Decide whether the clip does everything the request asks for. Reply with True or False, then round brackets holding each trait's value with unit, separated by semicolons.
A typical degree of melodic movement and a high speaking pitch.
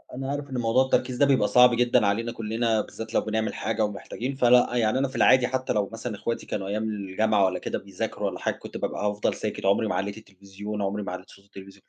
False (3.4 semitones; 110 Hz)